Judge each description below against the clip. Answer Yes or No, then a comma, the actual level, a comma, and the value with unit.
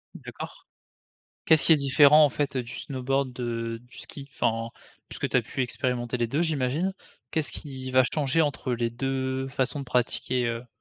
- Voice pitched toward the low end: Yes, low, 130 Hz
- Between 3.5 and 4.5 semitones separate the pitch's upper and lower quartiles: No, narrow, 2.5 semitones